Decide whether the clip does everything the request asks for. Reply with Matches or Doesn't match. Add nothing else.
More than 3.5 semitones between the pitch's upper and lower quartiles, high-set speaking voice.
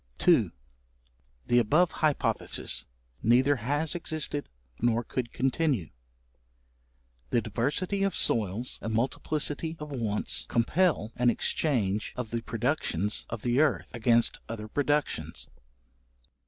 Doesn't match